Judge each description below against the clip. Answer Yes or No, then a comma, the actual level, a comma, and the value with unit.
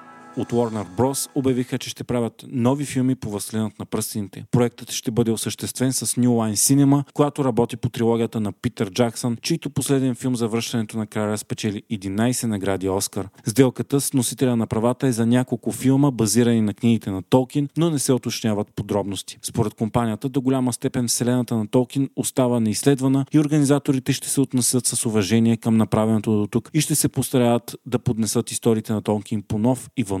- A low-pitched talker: Yes, low, 120 Hz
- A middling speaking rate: No, fast, 185 wpm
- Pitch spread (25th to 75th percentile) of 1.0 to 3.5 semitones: Yes, average, 2.9 semitones